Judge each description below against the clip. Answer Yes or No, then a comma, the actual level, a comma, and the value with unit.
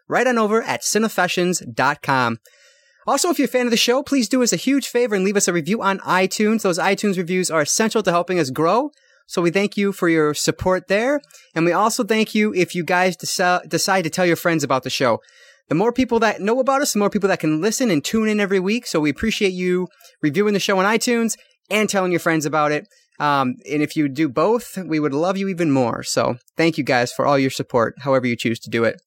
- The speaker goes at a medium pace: No, fast, 245 wpm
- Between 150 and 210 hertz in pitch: Yes, medium, 185 Hz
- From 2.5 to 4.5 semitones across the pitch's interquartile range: No, wide, 5.5 semitones